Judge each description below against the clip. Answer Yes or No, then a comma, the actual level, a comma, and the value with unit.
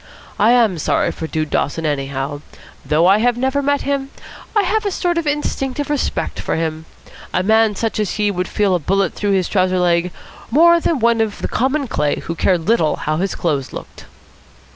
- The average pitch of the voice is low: No, high, 205 Hz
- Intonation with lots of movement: Yes, wide, 8.2 semitones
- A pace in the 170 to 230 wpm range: Yes, average, 195 wpm